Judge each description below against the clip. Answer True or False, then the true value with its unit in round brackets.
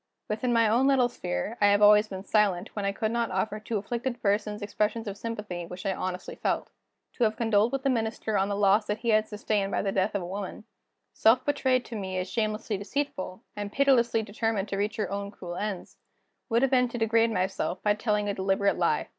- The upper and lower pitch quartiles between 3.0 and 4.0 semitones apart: False (2.5 semitones)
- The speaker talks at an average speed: False (220 wpm)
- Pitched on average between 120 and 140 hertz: False (210 Hz)